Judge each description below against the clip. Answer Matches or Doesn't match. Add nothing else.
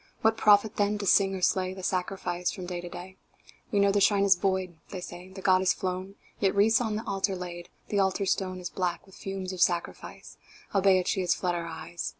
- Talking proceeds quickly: Matches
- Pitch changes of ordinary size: Doesn't match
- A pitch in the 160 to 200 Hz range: Matches